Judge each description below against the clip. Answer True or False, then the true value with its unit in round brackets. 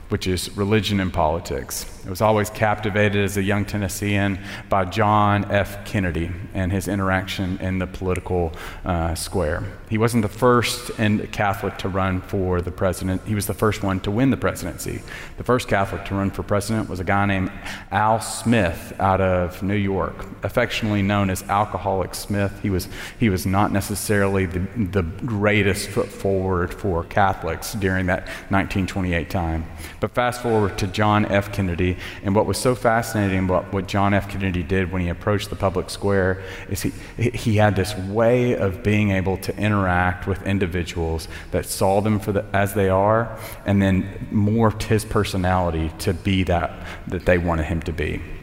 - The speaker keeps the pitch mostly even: True (2.1 semitones)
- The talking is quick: False (175 wpm)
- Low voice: True (100 Hz)